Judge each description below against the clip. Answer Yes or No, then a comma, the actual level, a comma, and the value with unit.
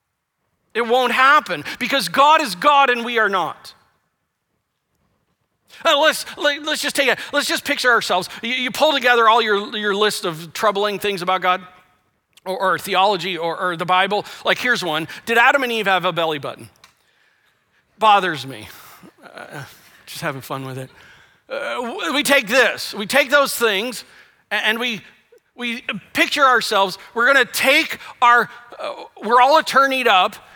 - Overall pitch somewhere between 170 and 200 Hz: No, high, 225 Hz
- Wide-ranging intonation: Yes, wide, 6.5 semitones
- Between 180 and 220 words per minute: No, average, 165 wpm